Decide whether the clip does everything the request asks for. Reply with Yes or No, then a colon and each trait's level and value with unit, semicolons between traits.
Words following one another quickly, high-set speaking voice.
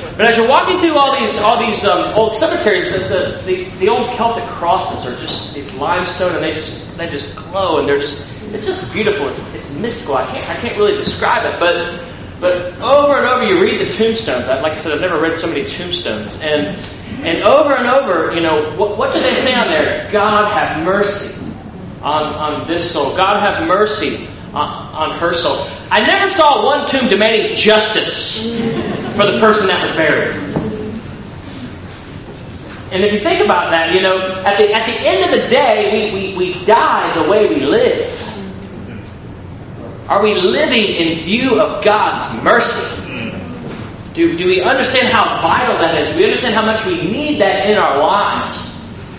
No: average, 190 wpm; high, 215 Hz